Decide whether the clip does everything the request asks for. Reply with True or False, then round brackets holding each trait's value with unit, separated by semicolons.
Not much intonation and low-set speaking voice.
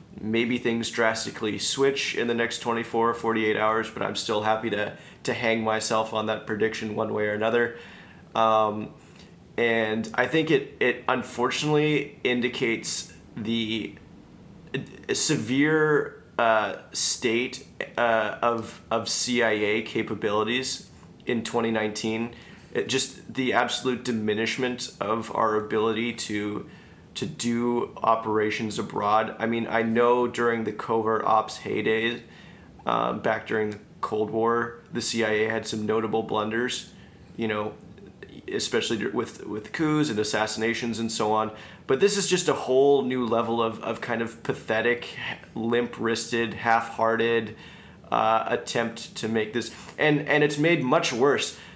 True (1.6 semitones; 115 Hz)